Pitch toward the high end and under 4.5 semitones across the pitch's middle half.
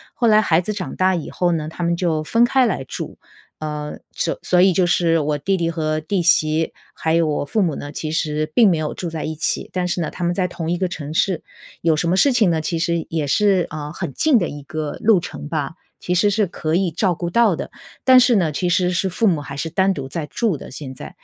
No: medium, 170 Hz; average, 3.4 semitones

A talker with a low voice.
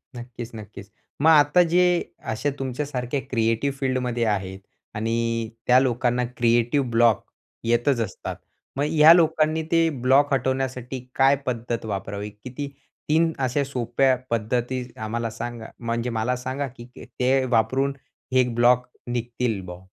Yes: low, 125 Hz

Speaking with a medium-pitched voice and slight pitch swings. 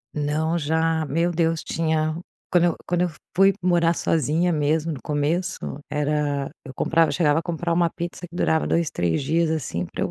Yes: medium, 160 Hz; narrow, 2.3 semitones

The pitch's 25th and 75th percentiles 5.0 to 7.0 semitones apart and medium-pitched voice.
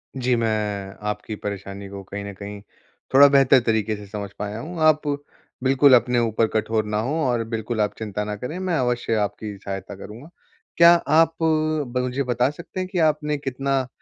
No: average, 5.3 semitones; low, 120 Hz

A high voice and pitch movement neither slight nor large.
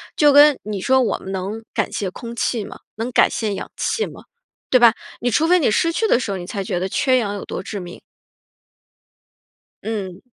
Yes: high, 225 Hz; average, 4.9 semitones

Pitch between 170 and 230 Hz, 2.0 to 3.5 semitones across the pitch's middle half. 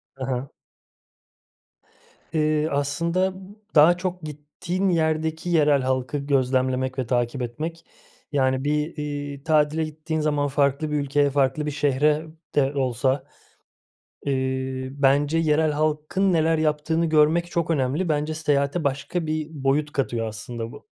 No: medium, 150 Hz; narrow, 2.6 semitones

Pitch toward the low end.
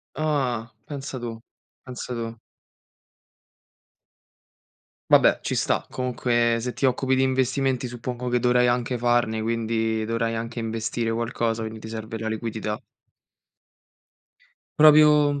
Yes: low, 120 Hz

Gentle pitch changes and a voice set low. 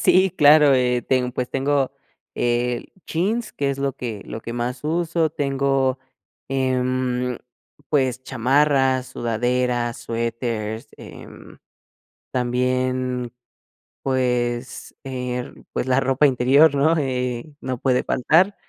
Yes: narrow, 2.0 semitones; low, 130 Hz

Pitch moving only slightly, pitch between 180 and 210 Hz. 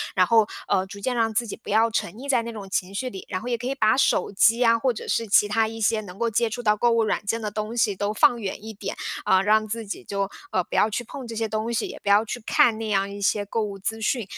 No: narrow, 2.2 semitones; high, 220 Hz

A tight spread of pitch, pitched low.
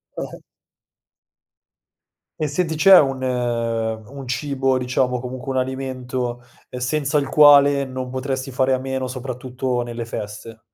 Yes: narrow, 1.6 semitones; low, 130 Hz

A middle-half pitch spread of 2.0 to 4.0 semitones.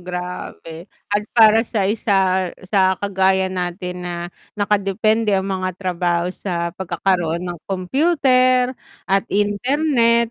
Yes: average, 3.3 semitones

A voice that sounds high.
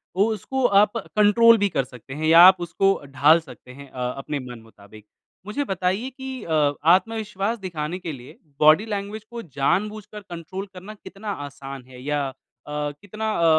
No: medium, 180 Hz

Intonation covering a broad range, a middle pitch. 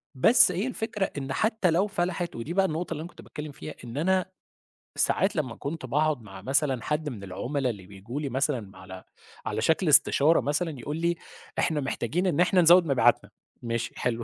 Yes: wide, 5.9 semitones; medium, 150 Hz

